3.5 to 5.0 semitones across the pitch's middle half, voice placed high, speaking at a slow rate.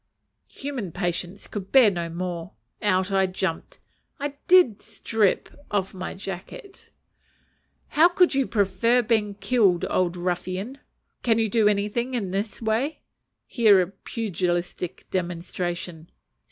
Yes: average, 4.2 semitones; high, 195 Hz; slow, 125 wpm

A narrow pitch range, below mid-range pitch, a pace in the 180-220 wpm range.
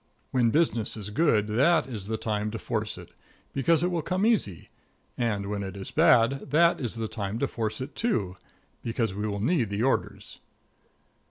No: average, 5.0 semitones; low, 115 Hz; average, 185 wpm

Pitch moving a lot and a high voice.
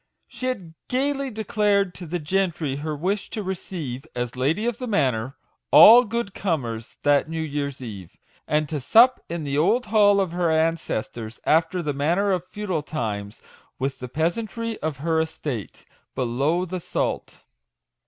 No: wide, 6.1 semitones; medium, 165 Hz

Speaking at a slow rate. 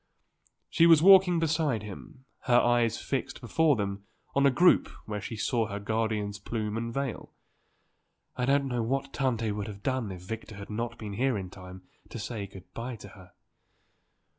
No: average, 180 wpm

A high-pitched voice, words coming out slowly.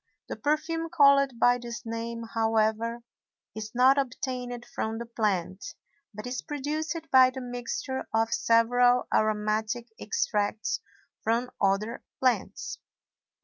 Yes: high, 235 Hz; slow, 115 wpm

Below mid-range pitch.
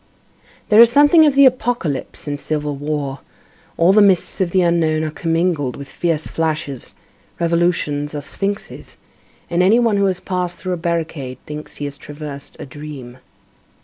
No: medium, 165 Hz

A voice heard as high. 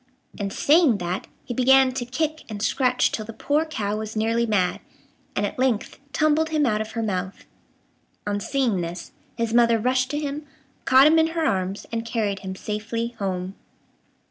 Yes: high, 230 Hz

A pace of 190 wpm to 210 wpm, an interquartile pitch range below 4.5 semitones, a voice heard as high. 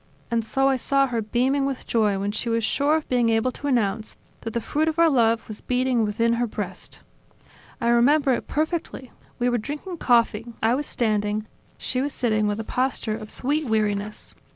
Yes: average, 200 wpm; average, 3.7 semitones; high, 235 Hz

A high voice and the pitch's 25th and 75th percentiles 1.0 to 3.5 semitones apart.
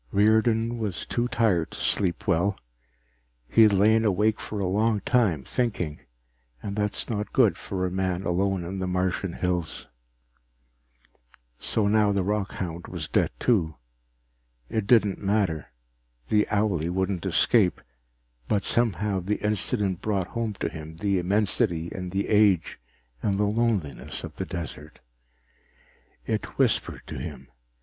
No: low, 100 Hz; average, 3.1 semitones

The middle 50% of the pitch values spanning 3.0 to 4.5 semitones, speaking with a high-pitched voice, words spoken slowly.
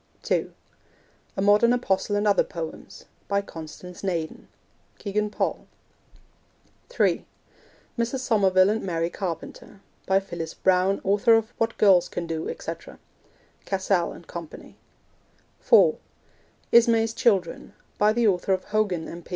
Yes: average, 3.5 semitones; high, 195 Hz; slow, 125 wpm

